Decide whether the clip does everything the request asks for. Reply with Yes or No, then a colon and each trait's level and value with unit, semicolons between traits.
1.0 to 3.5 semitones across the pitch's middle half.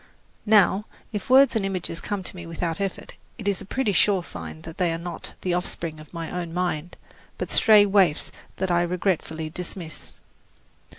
Yes: average, 3.1 semitones